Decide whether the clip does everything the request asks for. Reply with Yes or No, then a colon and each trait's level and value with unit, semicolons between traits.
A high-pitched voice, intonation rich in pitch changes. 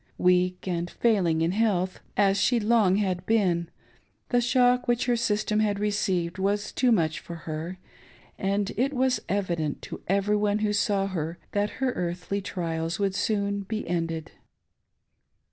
No: high, 200 Hz; average, 3.3 semitones